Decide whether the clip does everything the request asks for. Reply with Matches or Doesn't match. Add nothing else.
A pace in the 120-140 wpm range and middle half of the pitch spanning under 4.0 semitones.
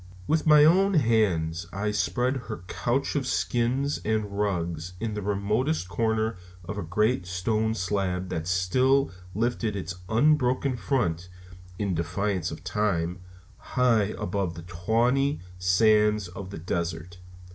Doesn't match